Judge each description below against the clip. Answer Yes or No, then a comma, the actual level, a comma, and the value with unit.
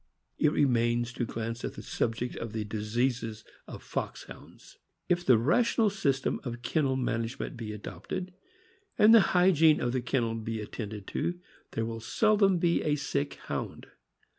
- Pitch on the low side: Yes, low, 125 Hz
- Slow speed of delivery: No, average, 155 wpm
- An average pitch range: No, wide, 5.9 semitones